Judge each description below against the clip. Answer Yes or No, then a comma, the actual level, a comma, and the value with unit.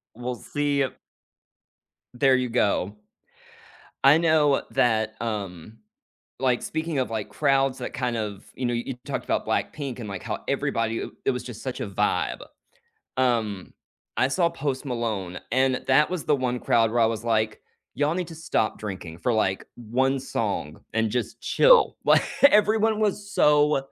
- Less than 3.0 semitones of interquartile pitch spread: No, average, 4.5 semitones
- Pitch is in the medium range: No, low, 125 Hz